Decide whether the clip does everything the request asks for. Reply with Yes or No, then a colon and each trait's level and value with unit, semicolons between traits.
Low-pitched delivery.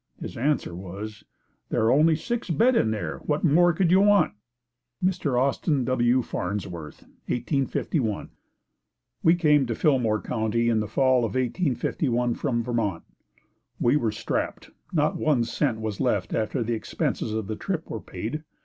Yes: low, 125 Hz